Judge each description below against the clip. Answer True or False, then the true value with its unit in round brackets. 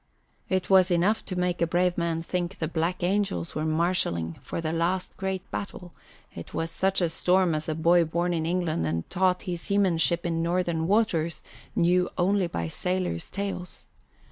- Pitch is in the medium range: True (175 Hz)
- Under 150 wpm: False (175 wpm)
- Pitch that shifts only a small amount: True (2.0 semitones)